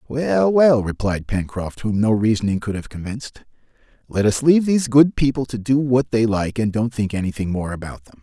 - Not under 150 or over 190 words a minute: No, fast, 205 wpm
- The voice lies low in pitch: Yes, low, 115 Hz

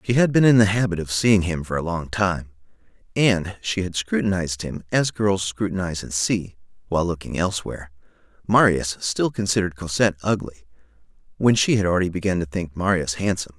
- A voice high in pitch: No, very low, 95 Hz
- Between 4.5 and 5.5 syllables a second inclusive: No, 6.0 syllables/s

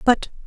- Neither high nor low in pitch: No, high, 245 Hz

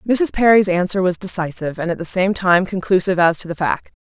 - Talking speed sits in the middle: No, fast, 225 wpm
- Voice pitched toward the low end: No, medium, 185 Hz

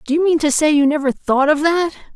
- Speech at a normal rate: No, fast, 280 wpm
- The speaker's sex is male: No, female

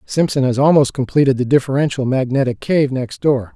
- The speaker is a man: Yes, male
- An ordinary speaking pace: Yes, average, 170 wpm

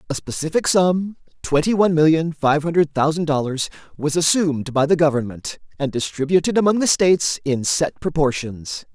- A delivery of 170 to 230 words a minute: No, average, 155 wpm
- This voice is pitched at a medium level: Yes, medium, 155 Hz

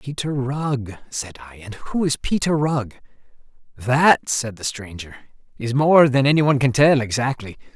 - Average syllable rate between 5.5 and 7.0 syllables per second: No, 4.5 syllables/s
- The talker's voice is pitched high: No, low, 130 Hz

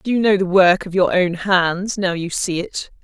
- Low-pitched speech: No, medium, 185 Hz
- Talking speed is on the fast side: Yes, fast, 255 wpm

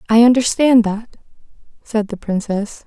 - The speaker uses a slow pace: Yes, slow, 125 wpm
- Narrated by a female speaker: Yes, female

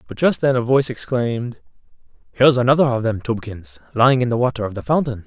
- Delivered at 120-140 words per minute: No, fast, 205 wpm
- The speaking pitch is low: Yes, low, 120 Hz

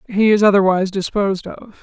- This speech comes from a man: No, female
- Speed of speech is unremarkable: Yes, average, 165 wpm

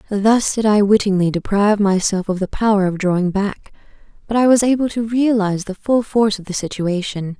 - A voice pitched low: No, high, 205 Hz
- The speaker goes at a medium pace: Yes, average, 195 wpm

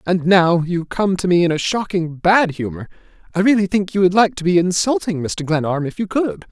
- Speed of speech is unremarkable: No, fast, 220 wpm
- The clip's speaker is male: Yes, male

